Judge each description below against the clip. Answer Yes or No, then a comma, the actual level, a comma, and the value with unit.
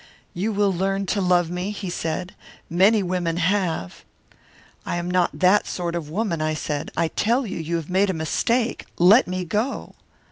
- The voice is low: No, medium, 180 Hz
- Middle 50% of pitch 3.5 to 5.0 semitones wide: No, average, 3.0 semitones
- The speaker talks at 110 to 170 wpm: No, average, 185 wpm